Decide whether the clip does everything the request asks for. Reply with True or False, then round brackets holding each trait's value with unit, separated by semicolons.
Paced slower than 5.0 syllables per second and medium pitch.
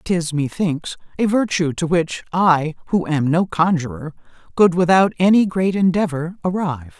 True (4.6 syllables/s; 170 Hz)